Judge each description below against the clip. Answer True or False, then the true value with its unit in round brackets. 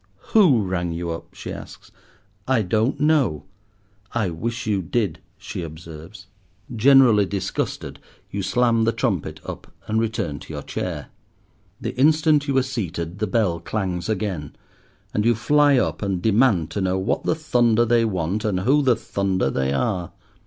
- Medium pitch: False (105 Hz)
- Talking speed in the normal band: True (160 wpm)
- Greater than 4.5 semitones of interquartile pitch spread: True (5.1 semitones)